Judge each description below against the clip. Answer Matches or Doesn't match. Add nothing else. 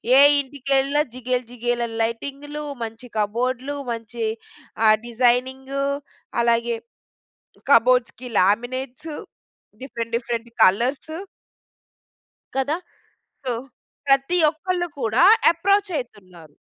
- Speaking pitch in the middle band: Doesn't match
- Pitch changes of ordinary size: Matches